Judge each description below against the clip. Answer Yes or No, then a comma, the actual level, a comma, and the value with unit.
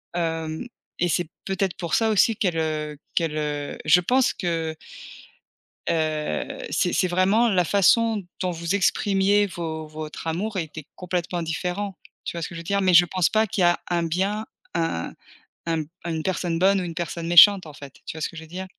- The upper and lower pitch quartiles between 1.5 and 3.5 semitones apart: Yes, average, 3.1 semitones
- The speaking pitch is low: No, medium, 175 Hz